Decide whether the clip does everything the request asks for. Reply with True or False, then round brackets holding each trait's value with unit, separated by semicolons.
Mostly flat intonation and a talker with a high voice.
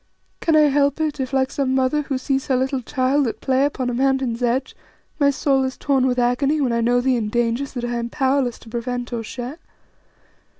True (2.1 semitones; 260 Hz)